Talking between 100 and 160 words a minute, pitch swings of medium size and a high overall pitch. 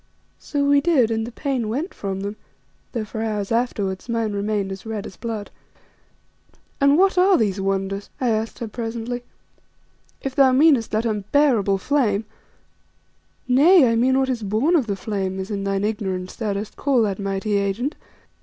No: average, 175 wpm; average, 4.5 semitones; high, 220 Hz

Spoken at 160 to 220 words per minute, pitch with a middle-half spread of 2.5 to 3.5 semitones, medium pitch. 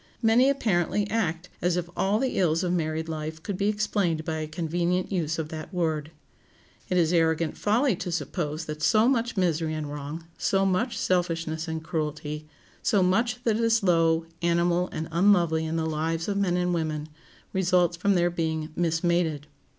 Yes: average, 175 wpm; average, 3.0 semitones; medium, 170 Hz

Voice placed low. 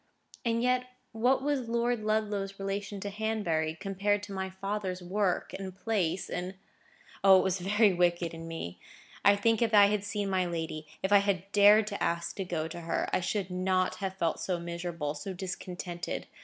No: high, 195 Hz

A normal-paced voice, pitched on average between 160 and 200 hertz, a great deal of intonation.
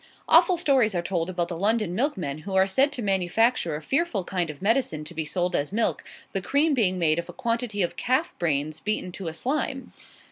No: fast, 215 wpm; high, 190 Hz; wide, 6.2 semitones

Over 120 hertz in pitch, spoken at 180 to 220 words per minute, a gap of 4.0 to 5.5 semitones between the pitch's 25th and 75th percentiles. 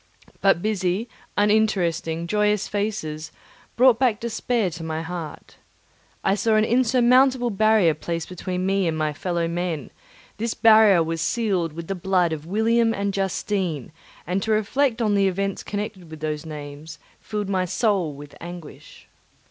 No: high, 190 Hz; average, 150 wpm; average, 4.6 semitones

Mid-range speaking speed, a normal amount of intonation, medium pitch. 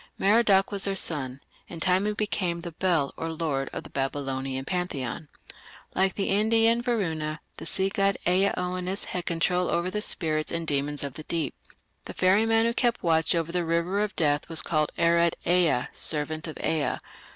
Yes: average, 180 wpm; average, 4.0 semitones; medium, 170 Hz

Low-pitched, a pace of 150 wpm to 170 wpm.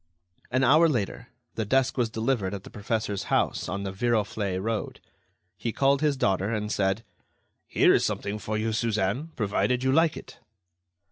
Yes: low, 110 Hz; average, 165 wpm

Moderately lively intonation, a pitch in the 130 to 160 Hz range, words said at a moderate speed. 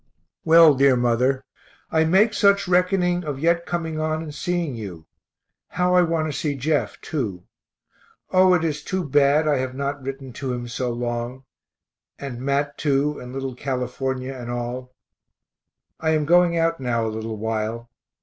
Yes: average, 4.7 semitones; medium, 140 Hz; average, 165 wpm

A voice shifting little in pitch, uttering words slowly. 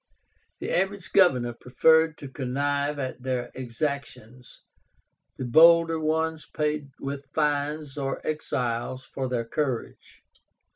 No: average, 3.4 semitones; slow, 110 wpm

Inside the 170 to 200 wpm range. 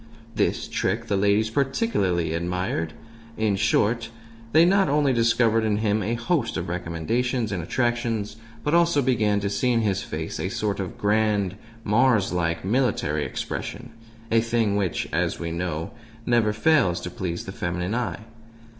No: average, 155 wpm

